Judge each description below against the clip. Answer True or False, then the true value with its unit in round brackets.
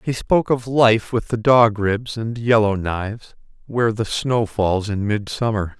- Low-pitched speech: True (110 Hz)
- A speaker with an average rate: True (175 wpm)